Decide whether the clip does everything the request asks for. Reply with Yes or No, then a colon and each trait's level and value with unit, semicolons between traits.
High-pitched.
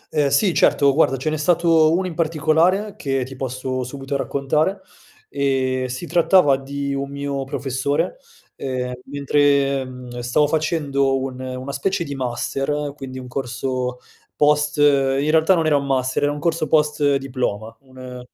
No: medium, 140 Hz